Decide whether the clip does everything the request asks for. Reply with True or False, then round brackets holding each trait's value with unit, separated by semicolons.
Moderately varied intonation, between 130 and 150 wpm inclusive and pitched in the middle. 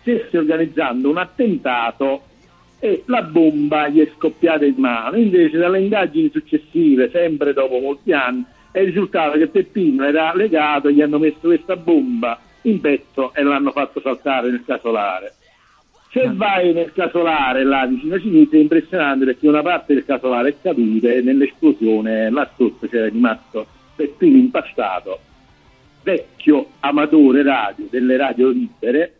False (6.1 semitones; 145 wpm; 155 Hz)